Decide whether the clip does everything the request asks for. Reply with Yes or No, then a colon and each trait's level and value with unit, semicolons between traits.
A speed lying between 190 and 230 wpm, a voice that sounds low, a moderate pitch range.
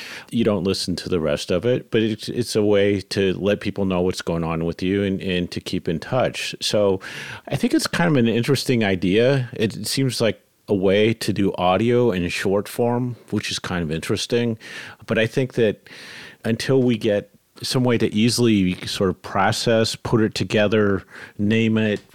Yes: average, 200 wpm; low, 110 Hz; average, 3.7 semitones